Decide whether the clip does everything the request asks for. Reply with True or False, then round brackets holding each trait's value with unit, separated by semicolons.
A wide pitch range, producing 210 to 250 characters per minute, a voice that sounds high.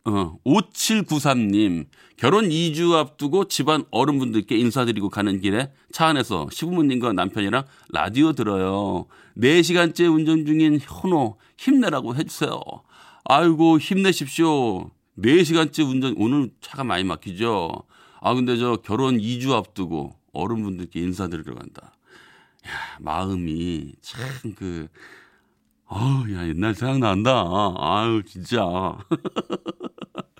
False (7.9 semitones; 245 characters per minute; 125 Hz)